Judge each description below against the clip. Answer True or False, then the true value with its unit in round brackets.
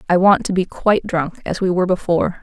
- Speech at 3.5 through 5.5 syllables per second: False (6.4 syllables/s)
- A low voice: False (180 Hz)